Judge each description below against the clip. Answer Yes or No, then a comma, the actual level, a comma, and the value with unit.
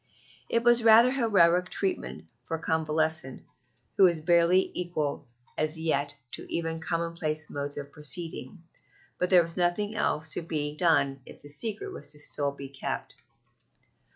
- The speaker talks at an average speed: Yes, average, 155 wpm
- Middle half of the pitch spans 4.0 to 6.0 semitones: No, average, 3.4 semitones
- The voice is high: No, medium, 165 Hz